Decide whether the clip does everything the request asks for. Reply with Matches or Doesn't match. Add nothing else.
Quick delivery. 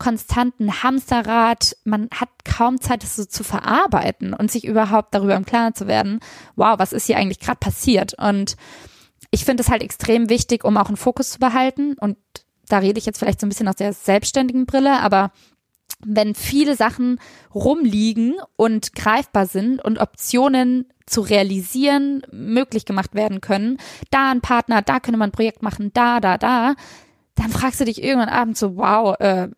Doesn't match